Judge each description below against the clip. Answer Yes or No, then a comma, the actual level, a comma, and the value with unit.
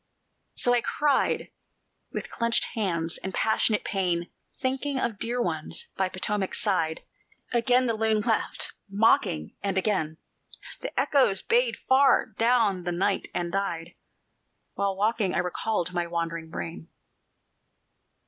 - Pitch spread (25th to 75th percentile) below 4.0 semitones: No, average, 5.1 semitones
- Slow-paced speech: Yes, slow, 130 wpm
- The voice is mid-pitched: No, high, 200 Hz